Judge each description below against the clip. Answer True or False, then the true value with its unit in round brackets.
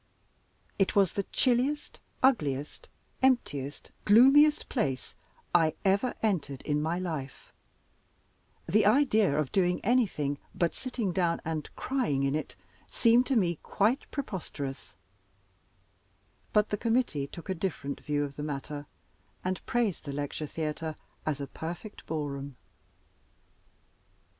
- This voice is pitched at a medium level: True (175 Hz)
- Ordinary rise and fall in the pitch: False (7.5 semitones)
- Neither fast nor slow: False (125 wpm)